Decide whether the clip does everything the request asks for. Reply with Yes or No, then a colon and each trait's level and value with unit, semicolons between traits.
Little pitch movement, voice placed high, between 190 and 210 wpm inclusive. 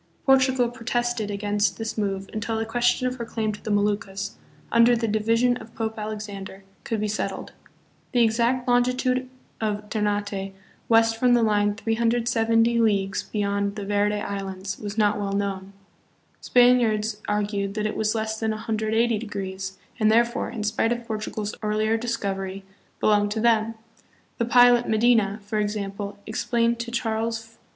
No: narrow, 2.2 semitones; high, 220 Hz; average, 160 wpm